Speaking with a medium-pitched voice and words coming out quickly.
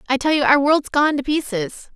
No: very high, 280 Hz; fast, 215 wpm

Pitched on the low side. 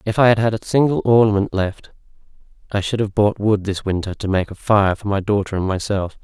Yes: low, 105 Hz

